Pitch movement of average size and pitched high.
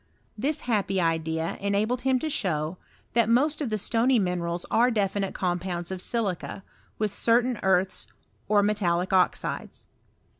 Yes: average, 4.5 semitones; high, 200 Hz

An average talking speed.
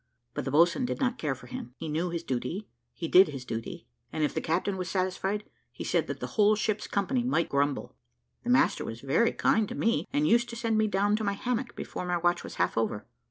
No: fast, 240 wpm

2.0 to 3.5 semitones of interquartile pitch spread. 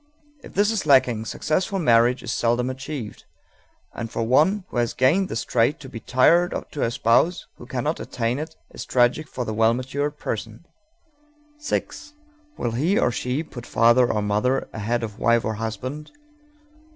No: average, 4.6 semitones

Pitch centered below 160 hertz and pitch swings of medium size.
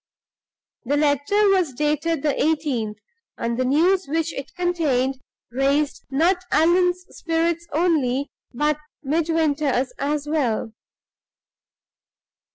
No: very high, 300 Hz; average, 3.5 semitones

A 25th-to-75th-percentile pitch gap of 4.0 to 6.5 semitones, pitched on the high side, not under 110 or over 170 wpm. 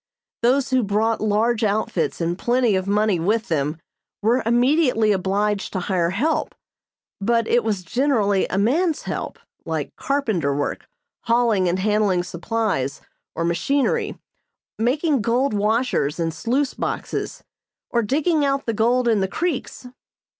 Yes: average, 4.6 semitones; high, 220 Hz; average, 140 wpm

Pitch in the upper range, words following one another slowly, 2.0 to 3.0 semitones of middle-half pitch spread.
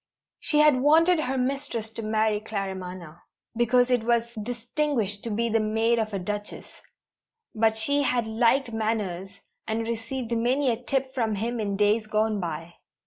No: high, 225 Hz; average, 160 wpm; average, 2.7 semitones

